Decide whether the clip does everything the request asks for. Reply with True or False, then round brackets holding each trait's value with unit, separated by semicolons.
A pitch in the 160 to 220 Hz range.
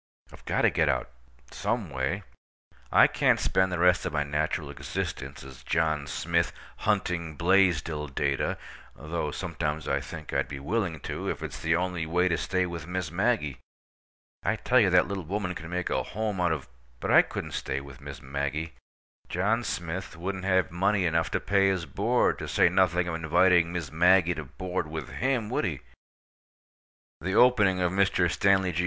False (85 Hz)